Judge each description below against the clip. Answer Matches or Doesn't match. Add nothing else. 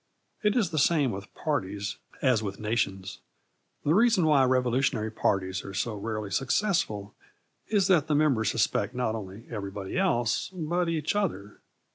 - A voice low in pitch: Matches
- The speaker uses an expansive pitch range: Matches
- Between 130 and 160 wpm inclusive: Matches